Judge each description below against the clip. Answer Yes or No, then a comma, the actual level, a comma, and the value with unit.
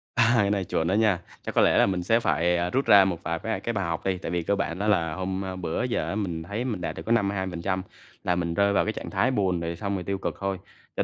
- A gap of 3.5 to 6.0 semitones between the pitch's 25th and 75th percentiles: No, average, 2.8 semitones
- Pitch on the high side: No, very low, 95 Hz